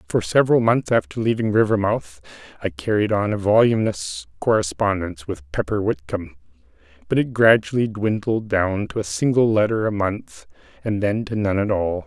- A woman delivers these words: No, male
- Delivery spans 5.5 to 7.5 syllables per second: No, 5.2 syllables/s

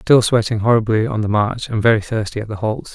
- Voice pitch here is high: No, low, 110 Hz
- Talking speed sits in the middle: No, fast, 245 wpm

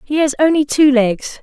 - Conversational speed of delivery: No, fast, 210 wpm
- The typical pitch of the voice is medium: No, very high, 280 Hz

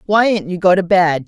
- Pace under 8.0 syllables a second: Yes, 4.4 syllables/s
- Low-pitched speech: No, medium, 185 Hz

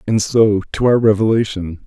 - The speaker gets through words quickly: No, average, 160 wpm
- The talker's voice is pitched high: No, low, 105 Hz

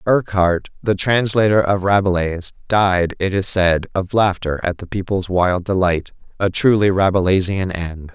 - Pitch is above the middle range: No, very low, 95 Hz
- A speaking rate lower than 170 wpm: Yes, average, 140 wpm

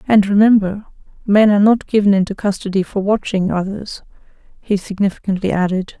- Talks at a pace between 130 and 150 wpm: Yes, average, 140 wpm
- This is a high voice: Yes, high, 200 Hz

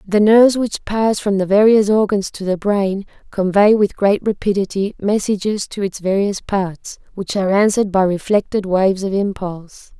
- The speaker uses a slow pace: No, average, 170 wpm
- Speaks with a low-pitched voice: No, high, 200 Hz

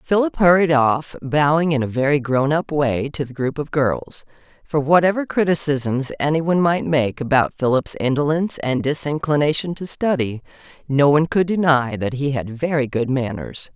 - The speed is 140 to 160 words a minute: No, average, 170 wpm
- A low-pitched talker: No, medium, 145 Hz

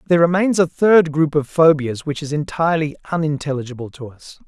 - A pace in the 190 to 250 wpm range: No, average, 175 wpm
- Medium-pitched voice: Yes, medium, 155 Hz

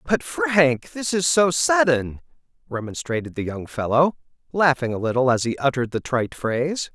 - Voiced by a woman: No, male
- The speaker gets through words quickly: No, average, 155 wpm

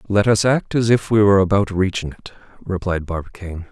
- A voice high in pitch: No, low, 100 Hz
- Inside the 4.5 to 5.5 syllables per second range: No, 5.9 syllables/s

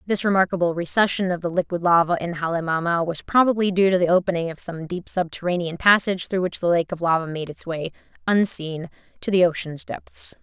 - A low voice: No, medium, 175 Hz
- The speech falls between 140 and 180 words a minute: No, average, 195 wpm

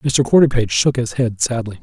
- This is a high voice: No, low, 120 Hz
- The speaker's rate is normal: Yes, average, 195 wpm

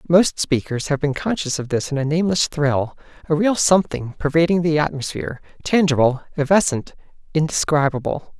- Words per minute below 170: Yes, average, 145 wpm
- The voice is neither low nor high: Yes, medium, 155 Hz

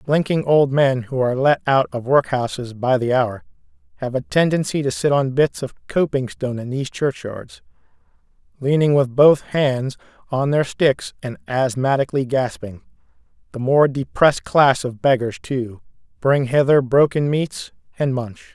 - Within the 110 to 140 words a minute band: No, average, 155 wpm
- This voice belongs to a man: Yes, male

